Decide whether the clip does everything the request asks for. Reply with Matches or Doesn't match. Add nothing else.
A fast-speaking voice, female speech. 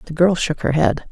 Matches